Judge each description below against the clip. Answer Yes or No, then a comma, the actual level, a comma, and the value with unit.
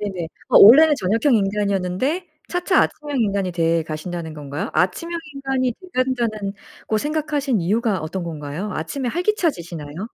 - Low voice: No, high, 210 Hz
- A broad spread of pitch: Yes, wide, 7.9 semitones